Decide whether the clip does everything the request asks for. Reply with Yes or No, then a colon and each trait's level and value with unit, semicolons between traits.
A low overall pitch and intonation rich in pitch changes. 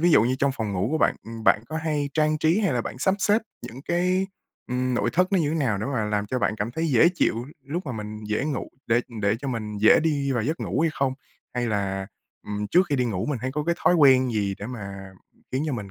Yes: low, 130 Hz; wide, 6.3 semitones